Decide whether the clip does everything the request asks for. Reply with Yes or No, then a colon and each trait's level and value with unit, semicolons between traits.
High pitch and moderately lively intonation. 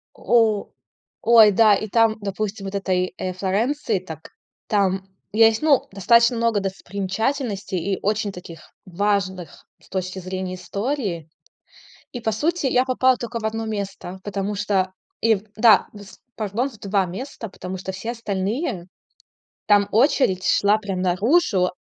Yes: high, 205 Hz; average, 3.1 semitones